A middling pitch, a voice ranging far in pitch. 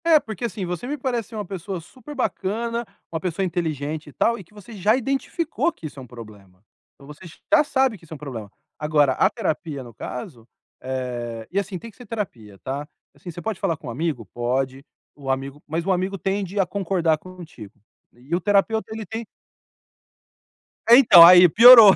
Yes: medium, 175 Hz; wide, 7.6 semitones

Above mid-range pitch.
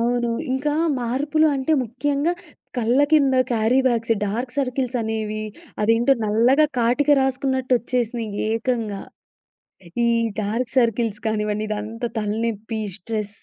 Yes: high, 235 Hz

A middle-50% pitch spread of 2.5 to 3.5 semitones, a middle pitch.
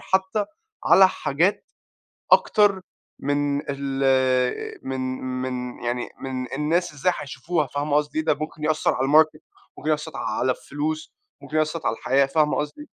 Yes: average, 2.8 semitones; medium, 150 Hz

